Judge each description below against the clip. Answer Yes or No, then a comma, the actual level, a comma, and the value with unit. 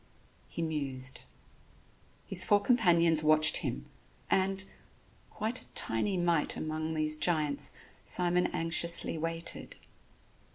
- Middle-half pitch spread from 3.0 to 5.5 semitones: No, narrow, 2.6 semitones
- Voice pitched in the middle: Yes, medium, 165 Hz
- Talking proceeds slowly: Yes, slow, 100 wpm